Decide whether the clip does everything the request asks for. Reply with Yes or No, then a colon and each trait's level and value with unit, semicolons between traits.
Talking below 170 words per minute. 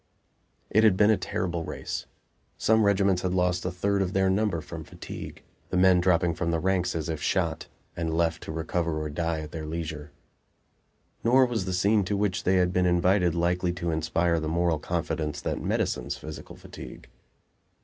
No: average, 185 wpm